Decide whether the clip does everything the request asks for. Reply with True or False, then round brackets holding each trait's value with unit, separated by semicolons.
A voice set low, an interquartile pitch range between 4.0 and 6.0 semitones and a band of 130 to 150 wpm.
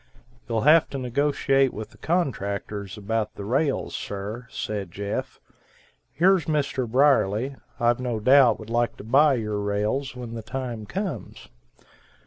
True (120 Hz; 4.5 semitones; 140 wpm)